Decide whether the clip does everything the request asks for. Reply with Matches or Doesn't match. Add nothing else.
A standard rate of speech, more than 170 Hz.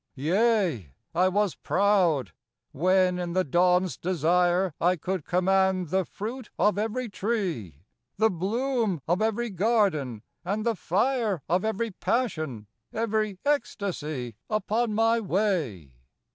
Doesn't match